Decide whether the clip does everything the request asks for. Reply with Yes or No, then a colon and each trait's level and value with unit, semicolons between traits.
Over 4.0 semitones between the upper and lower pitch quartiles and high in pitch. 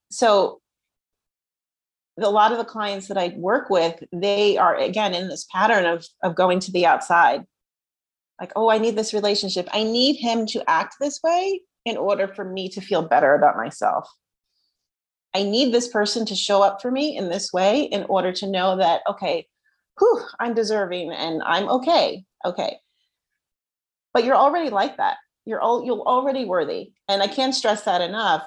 Yes: average, 5.2 semitones; high, 210 Hz